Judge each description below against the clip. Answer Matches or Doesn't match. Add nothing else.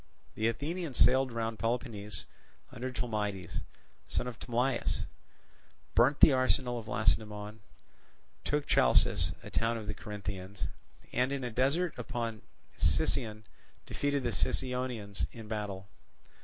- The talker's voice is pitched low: Matches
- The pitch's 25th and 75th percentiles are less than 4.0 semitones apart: Matches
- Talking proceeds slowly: Matches